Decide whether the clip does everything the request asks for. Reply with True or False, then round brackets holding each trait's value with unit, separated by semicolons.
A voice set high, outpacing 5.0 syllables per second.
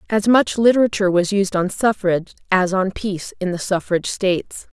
True (195 Hz; 5.6 syllables/s)